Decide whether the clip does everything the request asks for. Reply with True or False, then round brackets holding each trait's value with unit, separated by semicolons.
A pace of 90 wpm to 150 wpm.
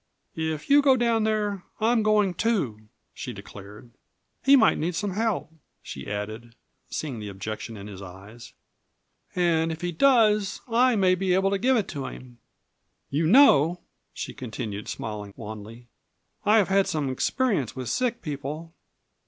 False (160 wpm)